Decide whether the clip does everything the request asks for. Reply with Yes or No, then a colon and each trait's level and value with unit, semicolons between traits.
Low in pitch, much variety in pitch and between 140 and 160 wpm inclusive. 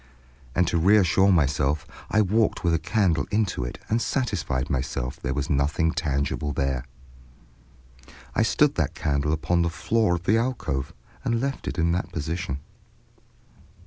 Yes: very low, 85 Hz; wide, 6.1 semitones; average, 155 wpm